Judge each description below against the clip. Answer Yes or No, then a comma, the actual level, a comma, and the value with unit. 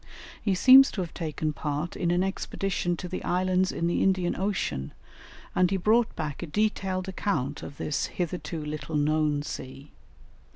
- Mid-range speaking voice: Yes, medium, 175 Hz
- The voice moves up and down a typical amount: Yes, average, 3.9 semitones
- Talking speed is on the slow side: No, average, 165 wpm